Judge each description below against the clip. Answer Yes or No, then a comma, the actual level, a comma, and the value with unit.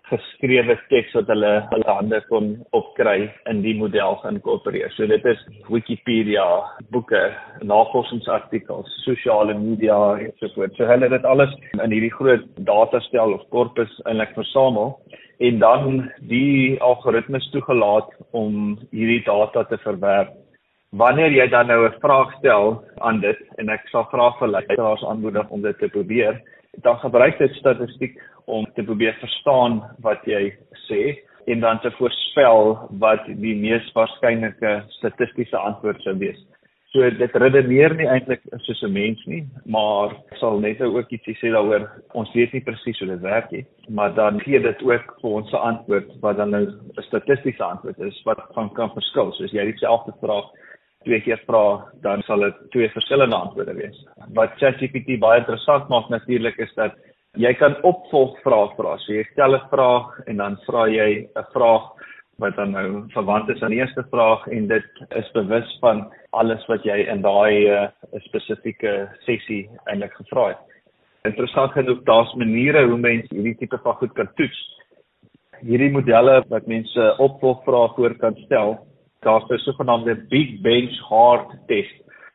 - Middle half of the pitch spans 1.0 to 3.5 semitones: Yes, average, 3.1 semitones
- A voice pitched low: Yes, low, 115 Hz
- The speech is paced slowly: No, average, 165 wpm